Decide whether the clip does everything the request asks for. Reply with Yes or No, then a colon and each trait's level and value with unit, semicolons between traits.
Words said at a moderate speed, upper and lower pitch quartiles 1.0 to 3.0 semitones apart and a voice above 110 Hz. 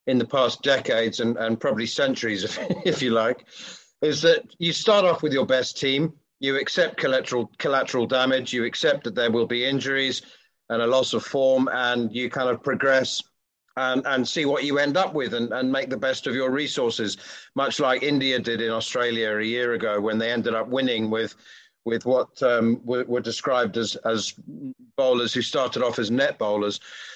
Yes: average, 195 wpm; average, 2.7 semitones; low, 125 Hz